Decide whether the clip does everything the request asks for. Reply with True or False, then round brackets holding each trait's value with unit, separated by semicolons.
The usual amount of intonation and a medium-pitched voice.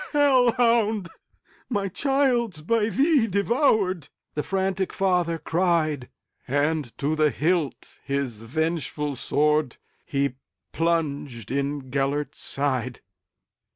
False (6.1 semitones; 160 Hz)